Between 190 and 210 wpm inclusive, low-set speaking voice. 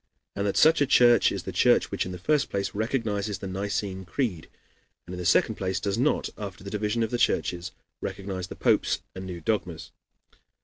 Yes: fast, 205 wpm; low, 100 Hz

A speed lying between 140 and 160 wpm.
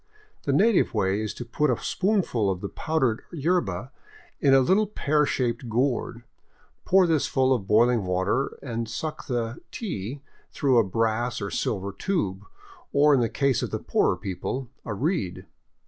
No: average, 175 wpm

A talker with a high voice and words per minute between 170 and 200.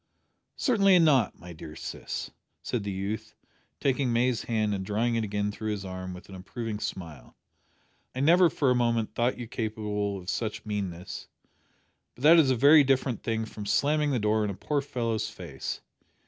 No: low, 110 Hz; average, 180 wpm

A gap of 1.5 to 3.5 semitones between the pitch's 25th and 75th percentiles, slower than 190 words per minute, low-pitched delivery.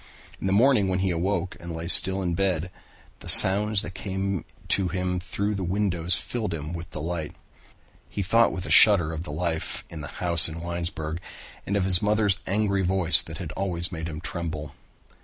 No: average, 2.8 semitones; average, 195 wpm; very low, 90 Hz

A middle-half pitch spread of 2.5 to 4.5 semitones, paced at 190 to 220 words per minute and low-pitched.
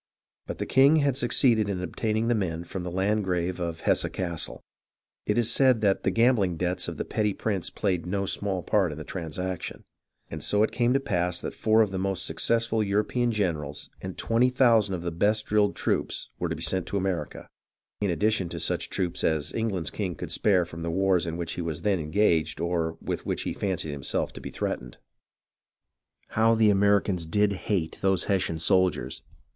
Yes: average, 3.8 semitones; average, 195 wpm; very low, 95 Hz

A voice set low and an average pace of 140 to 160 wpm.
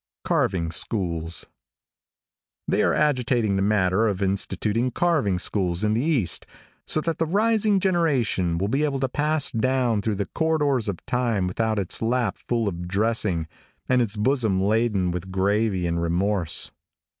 Yes: low, 110 Hz; average, 155 wpm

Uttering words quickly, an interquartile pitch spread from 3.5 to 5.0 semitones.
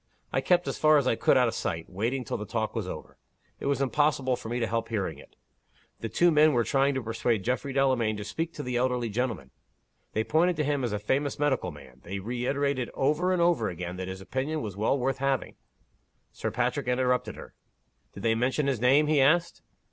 Yes: fast, 225 wpm; average, 4.2 semitones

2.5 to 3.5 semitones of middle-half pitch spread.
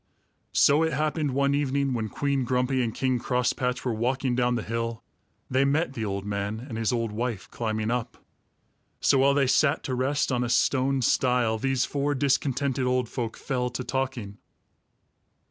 Yes: average, 2.8 semitones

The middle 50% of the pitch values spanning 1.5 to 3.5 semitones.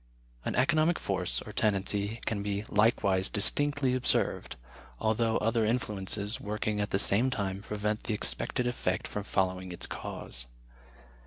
Yes: narrow, 2.6 semitones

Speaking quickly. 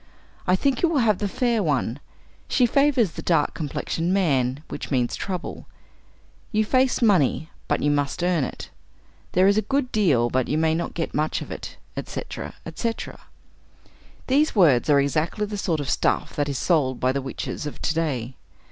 No: average, 185 wpm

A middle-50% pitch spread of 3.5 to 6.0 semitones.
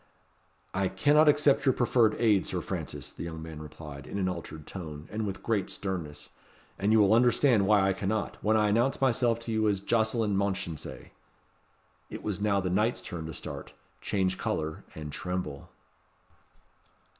Yes: average, 3.8 semitones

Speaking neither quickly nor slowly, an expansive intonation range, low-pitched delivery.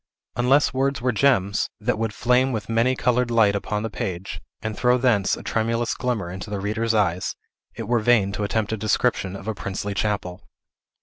No: average, 190 wpm; average, 3.3 semitones; low, 110 Hz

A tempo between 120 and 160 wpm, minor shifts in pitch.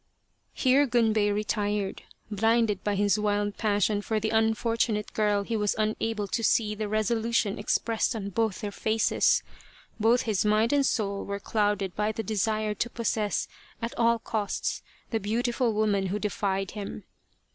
Yes: average, 155 wpm; narrow, 1.6 semitones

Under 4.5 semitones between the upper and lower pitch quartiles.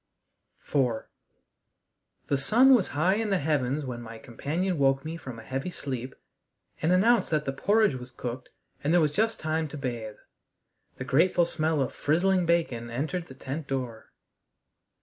No: average, 5.2 semitones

